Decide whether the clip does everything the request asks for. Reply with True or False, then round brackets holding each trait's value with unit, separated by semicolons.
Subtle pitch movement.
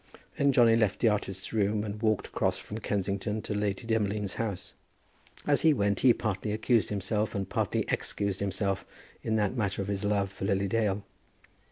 True (2.0 semitones)